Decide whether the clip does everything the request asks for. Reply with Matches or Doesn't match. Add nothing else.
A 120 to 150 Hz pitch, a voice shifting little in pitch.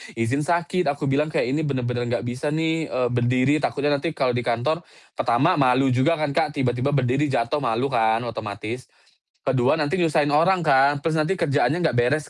Doesn't match